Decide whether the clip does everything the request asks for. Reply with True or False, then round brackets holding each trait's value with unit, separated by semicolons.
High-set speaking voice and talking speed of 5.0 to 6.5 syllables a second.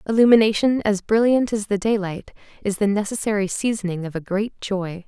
True (205 Hz; 5.5 syllables/s)